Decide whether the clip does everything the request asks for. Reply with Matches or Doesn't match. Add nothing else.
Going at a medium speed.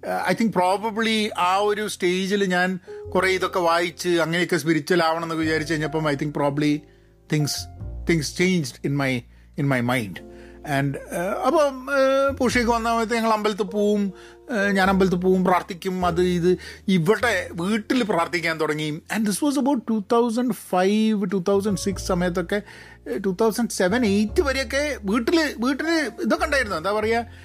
Doesn't match